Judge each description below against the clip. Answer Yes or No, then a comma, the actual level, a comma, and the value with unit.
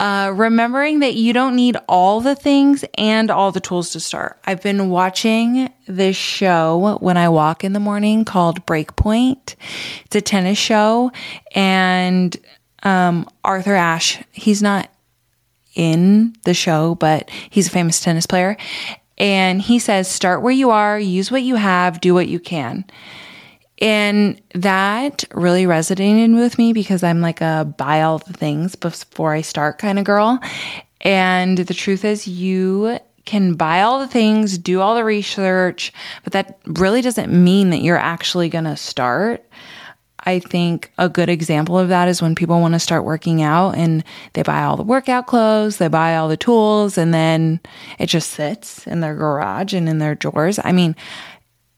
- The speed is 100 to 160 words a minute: No, average, 170 wpm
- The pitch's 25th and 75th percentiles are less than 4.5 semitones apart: Yes, average, 3.9 semitones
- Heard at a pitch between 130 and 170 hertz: No, medium, 185 Hz